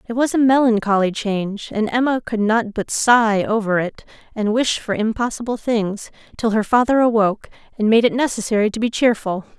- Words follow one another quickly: No, average, 180 wpm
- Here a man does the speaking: No, female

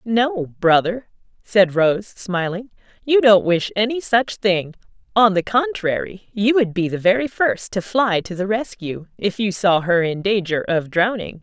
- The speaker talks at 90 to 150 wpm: No, average, 175 wpm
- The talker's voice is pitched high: Yes, high, 200 Hz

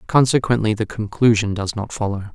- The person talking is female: No, male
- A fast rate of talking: No, average, 155 wpm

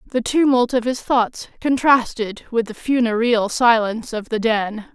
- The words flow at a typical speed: Yes, average, 160 wpm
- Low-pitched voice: No, high, 235 Hz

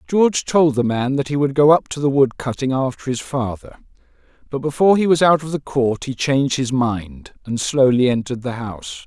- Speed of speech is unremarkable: No, fast, 220 wpm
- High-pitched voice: No, low, 135 Hz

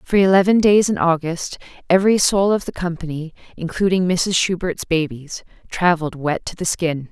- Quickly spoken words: No, average, 160 wpm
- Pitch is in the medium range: Yes, medium, 175 Hz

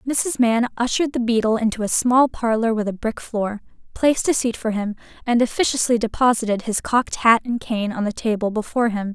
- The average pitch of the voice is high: Yes, high, 230 Hz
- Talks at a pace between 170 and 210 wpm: Yes, fast, 205 wpm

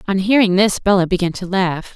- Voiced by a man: No, female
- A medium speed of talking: No, fast, 215 wpm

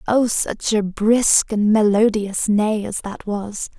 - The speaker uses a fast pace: No, average, 160 wpm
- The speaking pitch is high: Yes, high, 210 Hz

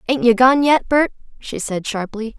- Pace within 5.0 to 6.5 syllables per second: No, 4.6 syllables/s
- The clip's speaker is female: Yes, female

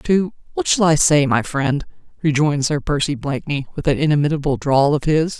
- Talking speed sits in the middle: Yes, average, 180 wpm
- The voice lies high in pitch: No, medium, 145 Hz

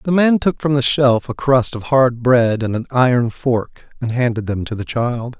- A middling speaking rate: No, fast, 235 wpm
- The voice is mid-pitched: No, low, 125 Hz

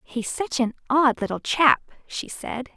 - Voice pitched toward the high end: Yes, very high, 260 Hz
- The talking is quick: No, average, 175 wpm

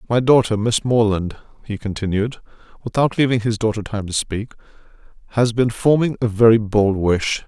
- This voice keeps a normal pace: Yes, average, 160 wpm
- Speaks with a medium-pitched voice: No, low, 110 Hz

